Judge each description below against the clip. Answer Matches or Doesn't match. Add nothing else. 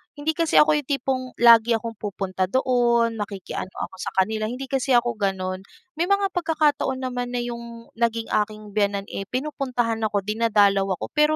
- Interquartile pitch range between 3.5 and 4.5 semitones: Matches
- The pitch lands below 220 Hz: Doesn't match